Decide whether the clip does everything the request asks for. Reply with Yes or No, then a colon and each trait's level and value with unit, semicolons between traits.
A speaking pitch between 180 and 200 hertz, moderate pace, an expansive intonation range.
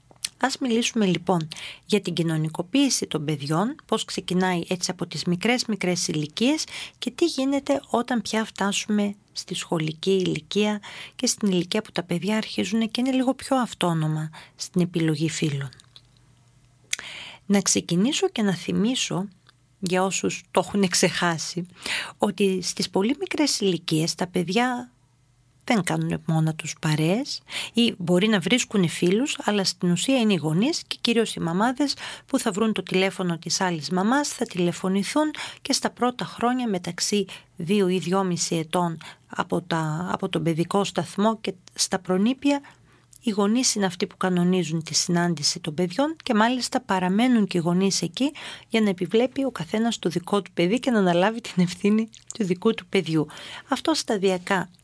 No: high, 190 Hz; average, 155 wpm; average, 4.6 semitones